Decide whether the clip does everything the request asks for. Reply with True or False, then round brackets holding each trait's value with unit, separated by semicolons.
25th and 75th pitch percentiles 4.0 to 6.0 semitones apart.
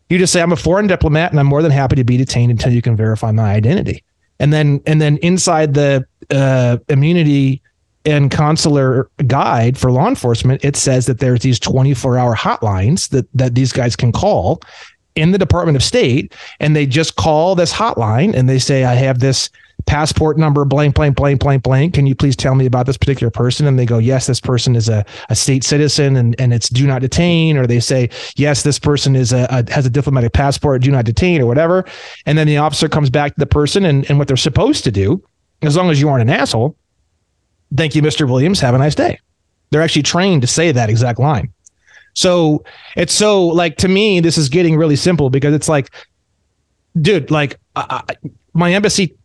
False (3.4 semitones)